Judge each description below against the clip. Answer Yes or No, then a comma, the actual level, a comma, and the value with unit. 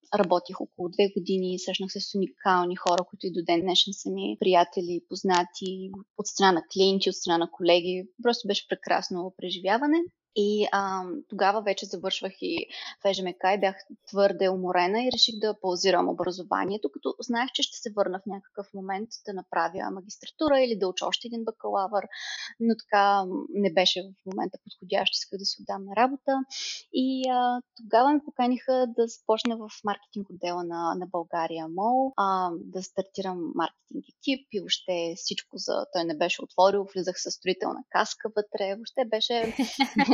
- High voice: Yes, high, 195 Hz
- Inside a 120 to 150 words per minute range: No, fast, 165 wpm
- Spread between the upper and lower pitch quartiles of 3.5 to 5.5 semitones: Yes, average, 3.8 semitones